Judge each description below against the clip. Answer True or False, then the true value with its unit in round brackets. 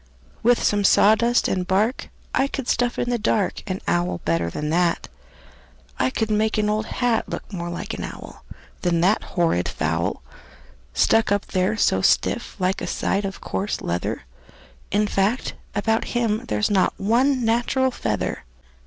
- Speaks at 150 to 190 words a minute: True (160 wpm)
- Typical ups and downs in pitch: True (4.8 semitones)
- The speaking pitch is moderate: False (205 Hz)